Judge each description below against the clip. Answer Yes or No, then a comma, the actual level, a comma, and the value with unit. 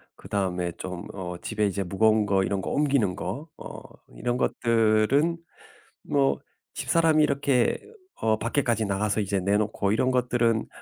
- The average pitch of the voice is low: Yes, low, 110 Hz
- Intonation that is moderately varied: Yes, average, 4.3 semitones